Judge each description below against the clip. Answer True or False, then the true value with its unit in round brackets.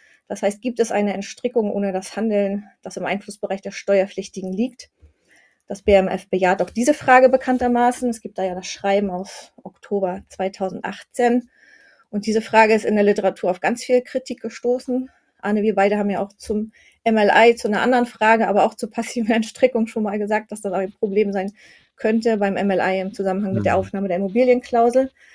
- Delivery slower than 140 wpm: False (185 wpm)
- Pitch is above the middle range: True (210 Hz)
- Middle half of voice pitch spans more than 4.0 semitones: False (3.4 semitones)